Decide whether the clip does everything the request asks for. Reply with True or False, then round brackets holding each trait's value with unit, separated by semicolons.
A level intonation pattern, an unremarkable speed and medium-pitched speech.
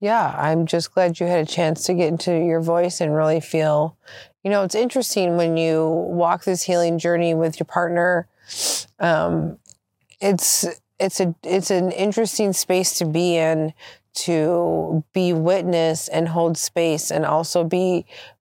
True (2.0 semitones; 160 wpm; 170 Hz)